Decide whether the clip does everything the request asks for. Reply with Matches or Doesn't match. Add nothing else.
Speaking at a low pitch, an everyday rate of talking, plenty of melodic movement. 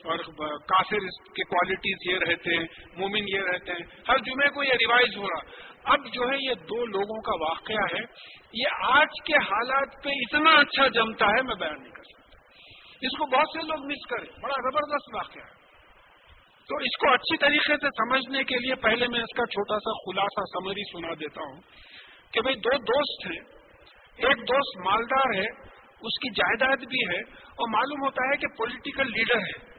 Doesn't match